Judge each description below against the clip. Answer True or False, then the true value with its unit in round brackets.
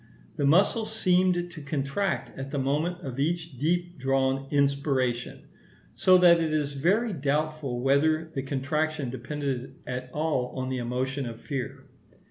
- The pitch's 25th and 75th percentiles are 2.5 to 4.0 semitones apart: True (3.7 semitones)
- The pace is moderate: True (145 wpm)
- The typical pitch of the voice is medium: True (145 Hz)